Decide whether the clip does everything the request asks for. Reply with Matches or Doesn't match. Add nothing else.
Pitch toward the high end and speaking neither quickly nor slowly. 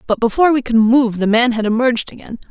Doesn't match